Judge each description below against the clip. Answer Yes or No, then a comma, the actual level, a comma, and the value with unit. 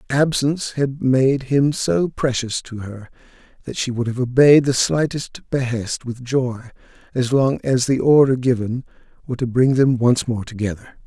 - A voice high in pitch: No, low, 125 Hz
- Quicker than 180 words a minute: No, average, 170 wpm